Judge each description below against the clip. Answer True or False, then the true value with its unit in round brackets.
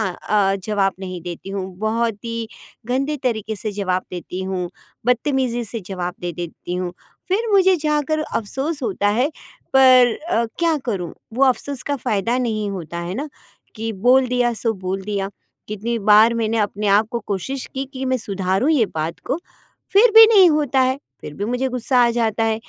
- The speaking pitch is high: True (225 Hz)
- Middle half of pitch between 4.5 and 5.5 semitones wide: True (5.1 semitones)